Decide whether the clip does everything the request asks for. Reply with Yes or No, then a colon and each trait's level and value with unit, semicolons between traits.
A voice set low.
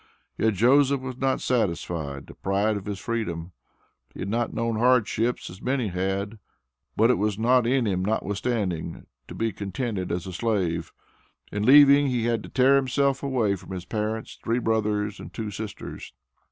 Yes: low, 110 Hz